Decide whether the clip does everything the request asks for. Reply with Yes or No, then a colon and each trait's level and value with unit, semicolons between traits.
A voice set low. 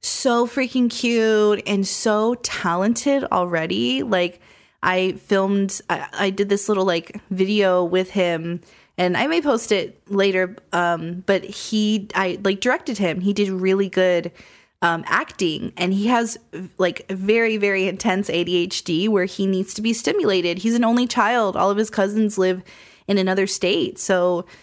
No: high, 195 Hz